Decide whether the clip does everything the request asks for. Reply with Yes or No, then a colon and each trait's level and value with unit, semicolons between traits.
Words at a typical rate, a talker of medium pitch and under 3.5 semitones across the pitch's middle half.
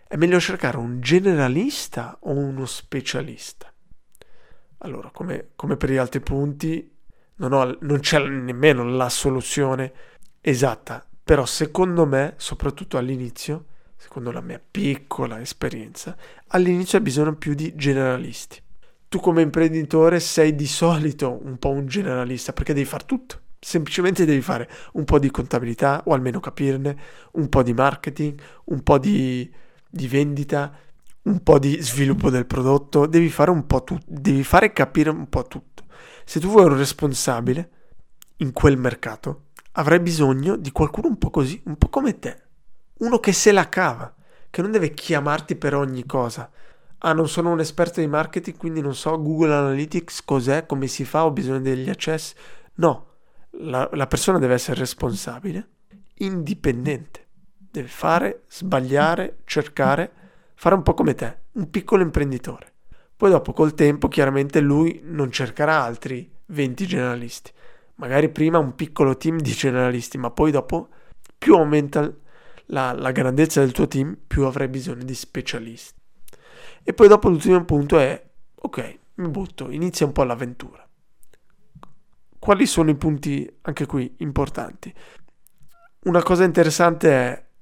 No: average, 150 wpm; medium, 150 Hz; average, 3.8 semitones